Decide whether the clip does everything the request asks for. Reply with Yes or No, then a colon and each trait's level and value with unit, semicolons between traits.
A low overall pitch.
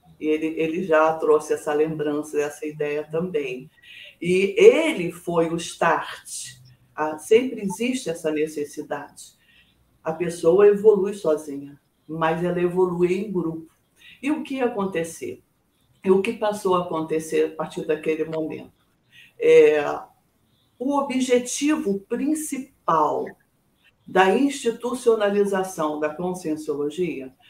No: medium, 170 Hz